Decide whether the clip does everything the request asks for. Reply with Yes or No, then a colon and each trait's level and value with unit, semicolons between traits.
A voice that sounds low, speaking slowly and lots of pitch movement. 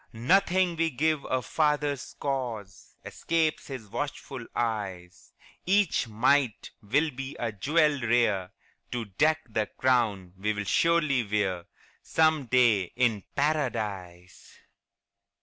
Yes: low, 125 Hz; slow, 110 wpm; wide, 6.2 semitones